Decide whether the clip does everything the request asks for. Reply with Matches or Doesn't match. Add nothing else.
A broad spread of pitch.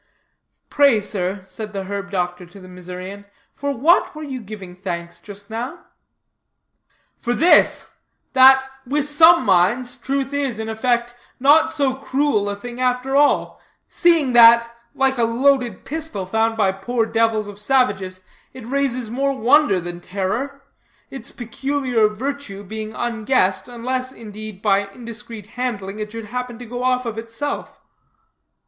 Doesn't match